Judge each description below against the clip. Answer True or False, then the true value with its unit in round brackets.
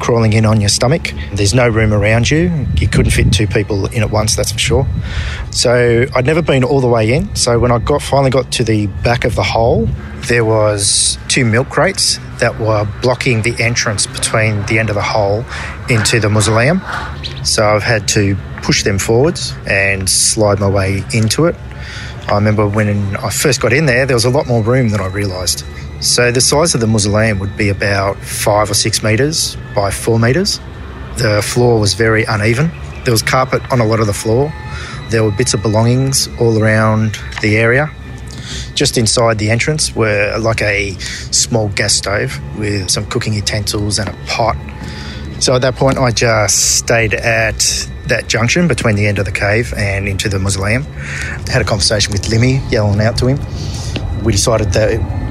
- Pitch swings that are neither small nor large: True (3.1 semitones)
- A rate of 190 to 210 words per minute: True (195 wpm)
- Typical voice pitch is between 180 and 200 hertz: False (110 Hz)